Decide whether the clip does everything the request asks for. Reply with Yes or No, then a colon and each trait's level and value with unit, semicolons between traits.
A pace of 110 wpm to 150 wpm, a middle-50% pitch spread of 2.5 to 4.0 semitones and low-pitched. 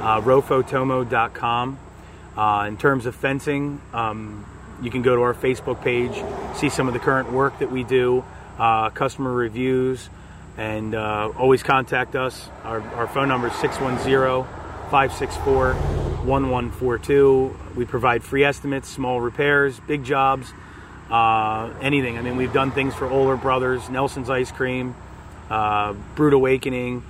Yes: average, 140 wpm; average, 3.5 semitones; low, 125 Hz